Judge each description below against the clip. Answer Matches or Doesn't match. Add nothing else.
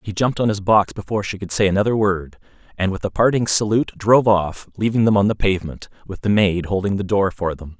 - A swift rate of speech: Matches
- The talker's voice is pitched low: Matches